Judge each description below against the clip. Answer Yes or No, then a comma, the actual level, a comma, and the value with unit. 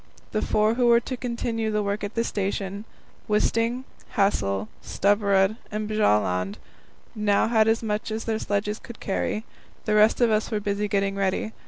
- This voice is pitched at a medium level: No, high, 210 Hz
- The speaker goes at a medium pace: Yes, average, 170 wpm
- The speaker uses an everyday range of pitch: No, narrow, 1.9 semitones